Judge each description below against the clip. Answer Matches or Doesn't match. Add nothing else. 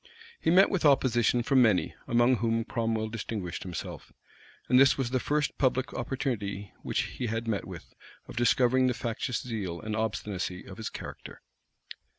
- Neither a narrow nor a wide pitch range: Matches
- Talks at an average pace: Matches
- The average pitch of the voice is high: Doesn't match